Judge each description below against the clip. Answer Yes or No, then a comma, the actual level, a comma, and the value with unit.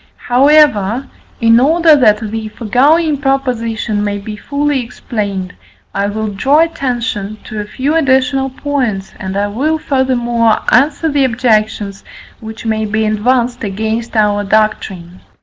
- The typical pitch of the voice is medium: No, high, 230 Hz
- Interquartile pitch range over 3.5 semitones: Yes, average, 4.3 semitones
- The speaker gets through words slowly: Yes, slow, 130 wpm